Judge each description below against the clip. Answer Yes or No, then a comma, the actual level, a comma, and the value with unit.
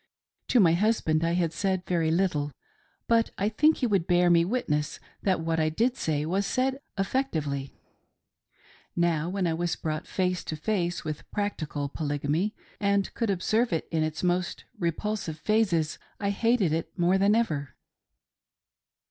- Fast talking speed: No, average, 155 wpm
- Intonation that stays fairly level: No, average, 4.4 semitones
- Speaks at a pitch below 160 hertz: No, medium, 175 Hz